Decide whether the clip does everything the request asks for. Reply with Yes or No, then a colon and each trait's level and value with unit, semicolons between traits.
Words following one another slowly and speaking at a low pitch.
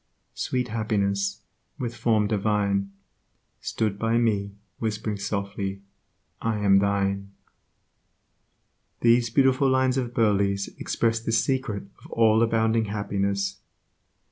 Yes: slow, 105 wpm; low, 105 Hz